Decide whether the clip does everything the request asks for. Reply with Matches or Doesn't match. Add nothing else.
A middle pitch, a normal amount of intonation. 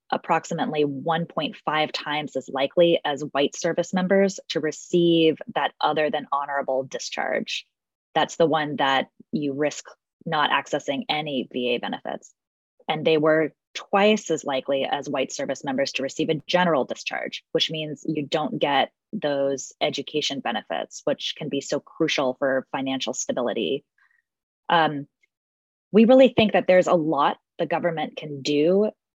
Matches